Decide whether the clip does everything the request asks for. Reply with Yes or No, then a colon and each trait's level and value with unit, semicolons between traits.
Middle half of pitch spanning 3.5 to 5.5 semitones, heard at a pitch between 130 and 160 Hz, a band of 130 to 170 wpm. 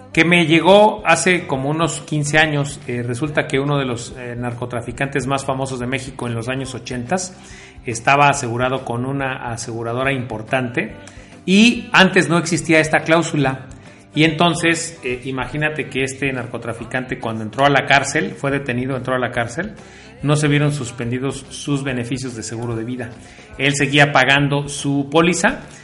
Yes: average, 4.1 semitones; low, 135 Hz; average, 160 wpm